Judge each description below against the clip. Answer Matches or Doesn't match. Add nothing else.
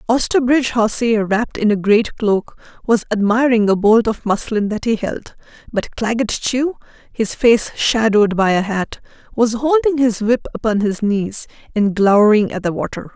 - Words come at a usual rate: Matches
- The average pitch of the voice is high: Matches